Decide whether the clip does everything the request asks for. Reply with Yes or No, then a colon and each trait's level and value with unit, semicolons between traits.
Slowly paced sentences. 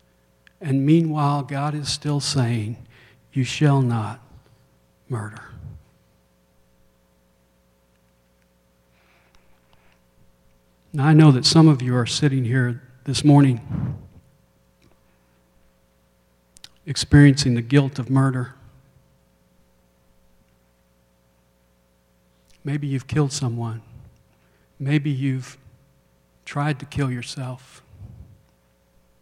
Yes: slow, 75 wpm